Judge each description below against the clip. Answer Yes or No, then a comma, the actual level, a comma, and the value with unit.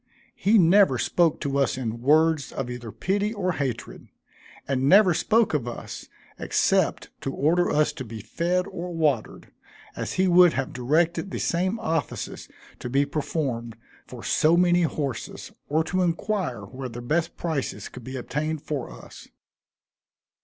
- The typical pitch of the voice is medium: Yes, medium, 155 Hz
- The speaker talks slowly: No, average, 155 wpm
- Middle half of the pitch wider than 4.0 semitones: Yes, average, 5.2 semitones